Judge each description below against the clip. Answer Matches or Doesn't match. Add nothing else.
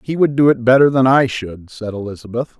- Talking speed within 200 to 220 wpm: Doesn't match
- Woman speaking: Doesn't match